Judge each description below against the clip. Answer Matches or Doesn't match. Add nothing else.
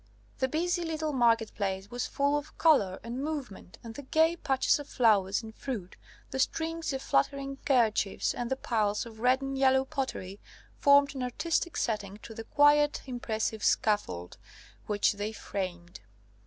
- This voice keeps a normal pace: Matches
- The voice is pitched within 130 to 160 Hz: Doesn't match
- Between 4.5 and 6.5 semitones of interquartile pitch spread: Matches